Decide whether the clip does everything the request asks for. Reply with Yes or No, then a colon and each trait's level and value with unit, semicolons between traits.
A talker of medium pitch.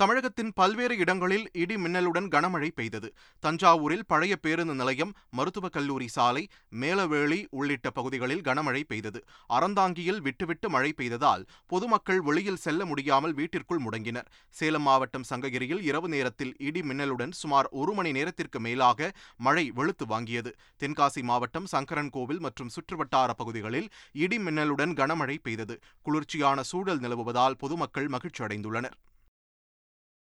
Yes: medium, 145 Hz